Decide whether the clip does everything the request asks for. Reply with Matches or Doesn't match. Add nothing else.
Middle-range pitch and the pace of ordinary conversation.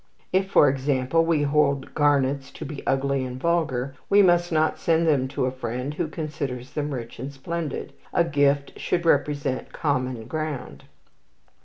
Matches